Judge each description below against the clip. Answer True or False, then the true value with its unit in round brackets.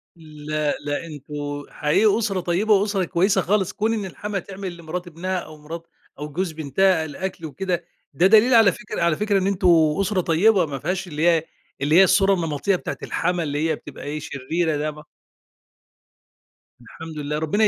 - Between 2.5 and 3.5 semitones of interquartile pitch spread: False (4.1 semitones)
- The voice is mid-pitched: True (170 Hz)